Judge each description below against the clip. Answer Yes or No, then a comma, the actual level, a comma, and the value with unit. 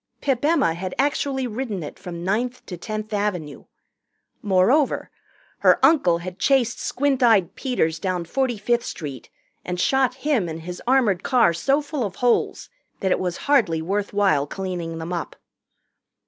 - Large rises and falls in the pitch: Yes, wide, 6.7 semitones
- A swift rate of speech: No, average, 160 wpm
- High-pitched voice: Yes, high, 205 Hz